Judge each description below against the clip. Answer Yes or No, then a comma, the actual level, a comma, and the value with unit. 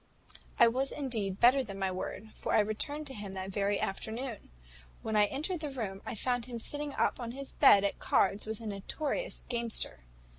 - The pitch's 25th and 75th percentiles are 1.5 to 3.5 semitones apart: No, average, 5.0 semitones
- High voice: Yes, high, 230 Hz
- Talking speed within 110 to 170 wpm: No, average, 195 wpm